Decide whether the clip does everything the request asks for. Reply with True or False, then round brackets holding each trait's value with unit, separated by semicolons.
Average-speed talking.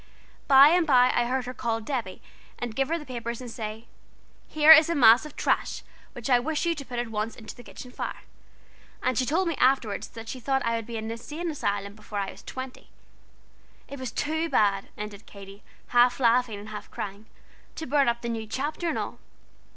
False (215 wpm)